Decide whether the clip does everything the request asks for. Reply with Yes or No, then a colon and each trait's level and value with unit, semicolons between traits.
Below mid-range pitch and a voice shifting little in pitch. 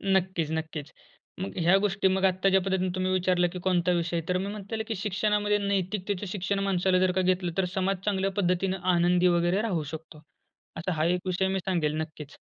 No: medium, 185 Hz; narrow, 1.7 semitones